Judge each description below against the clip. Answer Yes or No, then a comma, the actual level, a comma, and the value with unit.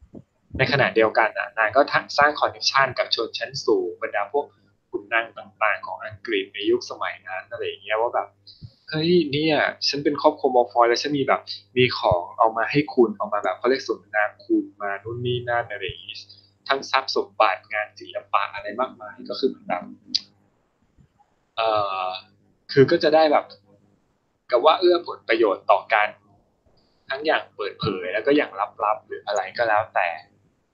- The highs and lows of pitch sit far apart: Yes, wide, 8.2 semitones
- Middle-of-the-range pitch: Yes, medium, 145 Hz